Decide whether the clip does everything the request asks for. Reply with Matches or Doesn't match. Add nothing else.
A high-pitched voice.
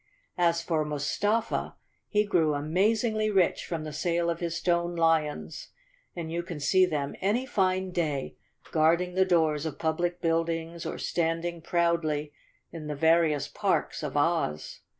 Doesn't match